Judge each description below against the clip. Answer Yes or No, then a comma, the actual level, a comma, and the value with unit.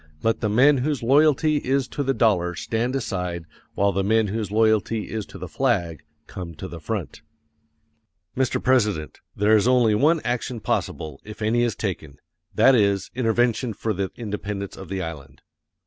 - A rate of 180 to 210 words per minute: No, average, 170 wpm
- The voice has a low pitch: Yes, low, 110 Hz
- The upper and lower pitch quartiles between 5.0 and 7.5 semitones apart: No, average, 4.1 semitones